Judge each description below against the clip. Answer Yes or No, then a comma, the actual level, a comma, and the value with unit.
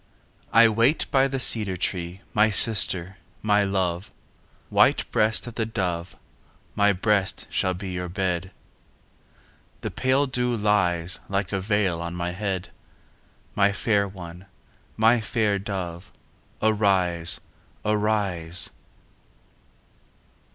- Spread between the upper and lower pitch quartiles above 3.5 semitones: No, average, 3.1 semitones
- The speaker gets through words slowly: Yes, slow, 115 wpm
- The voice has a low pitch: Yes, low, 100 Hz